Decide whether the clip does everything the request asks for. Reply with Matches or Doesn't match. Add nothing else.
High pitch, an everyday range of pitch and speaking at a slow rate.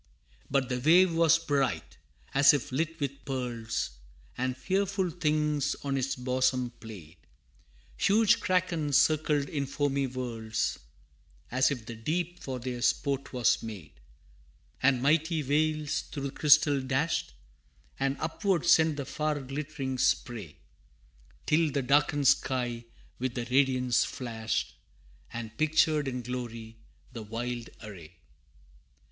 Doesn't match